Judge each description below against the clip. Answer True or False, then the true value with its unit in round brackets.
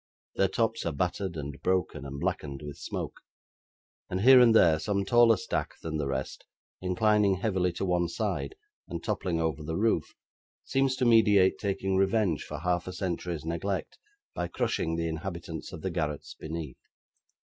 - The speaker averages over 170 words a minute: False (165 wpm)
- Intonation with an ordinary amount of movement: True (3.8 semitones)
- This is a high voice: False (90 Hz)